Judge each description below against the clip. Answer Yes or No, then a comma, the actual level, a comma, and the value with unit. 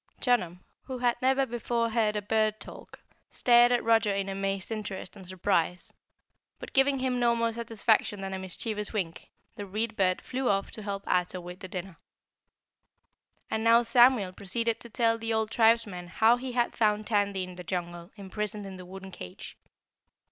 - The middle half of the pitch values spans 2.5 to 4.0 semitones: Yes, average, 3.4 semitones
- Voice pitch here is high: Yes, high, 210 Hz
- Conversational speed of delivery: Yes, average, 175 wpm